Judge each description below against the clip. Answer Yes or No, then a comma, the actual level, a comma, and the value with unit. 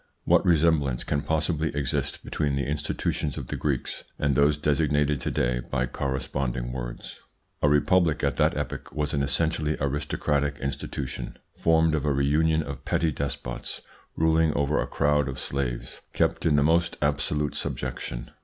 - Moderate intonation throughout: No, narrow, 1.9 semitones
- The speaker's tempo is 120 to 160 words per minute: Yes, average, 155 wpm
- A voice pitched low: Yes, very low, 75 Hz